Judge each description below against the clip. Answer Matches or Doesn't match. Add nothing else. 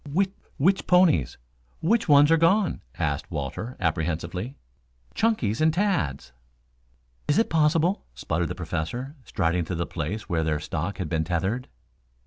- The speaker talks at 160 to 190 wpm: Doesn't match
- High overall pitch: Doesn't match